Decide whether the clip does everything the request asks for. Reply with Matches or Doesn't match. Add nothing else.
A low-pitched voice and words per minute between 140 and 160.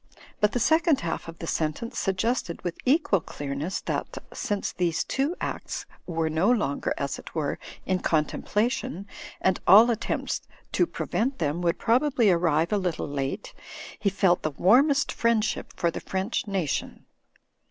Doesn't match